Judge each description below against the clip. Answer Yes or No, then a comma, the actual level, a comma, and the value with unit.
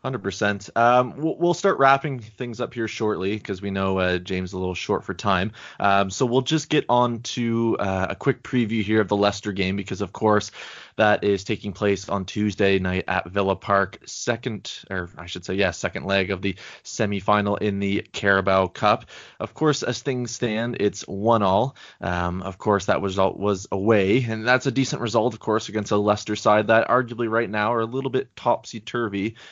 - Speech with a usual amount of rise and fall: Yes, average, 3.3 semitones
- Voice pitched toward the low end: Yes, low, 105 Hz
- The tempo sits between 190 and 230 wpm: Yes, fast, 205 wpm